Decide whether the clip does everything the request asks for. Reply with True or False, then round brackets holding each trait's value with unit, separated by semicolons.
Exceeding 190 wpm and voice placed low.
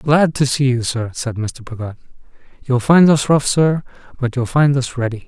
True (205 wpm; 130 Hz)